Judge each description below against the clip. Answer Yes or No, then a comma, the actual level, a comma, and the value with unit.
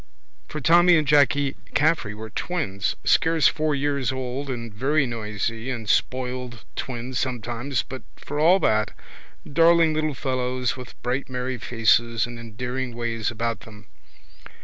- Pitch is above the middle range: No, low, 125 Hz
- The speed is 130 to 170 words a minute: Yes, average, 140 wpm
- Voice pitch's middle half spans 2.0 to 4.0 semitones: Yes, average, 3.6 semitones